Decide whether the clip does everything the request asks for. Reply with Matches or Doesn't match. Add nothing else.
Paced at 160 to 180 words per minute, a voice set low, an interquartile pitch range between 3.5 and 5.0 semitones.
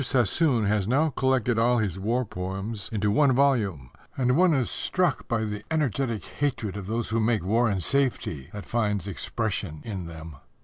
Matches